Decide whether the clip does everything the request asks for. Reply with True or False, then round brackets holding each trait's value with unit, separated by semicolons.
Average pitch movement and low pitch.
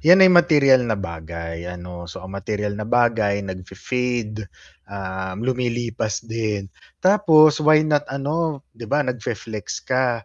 False (5.9 semitones; 115 Hz)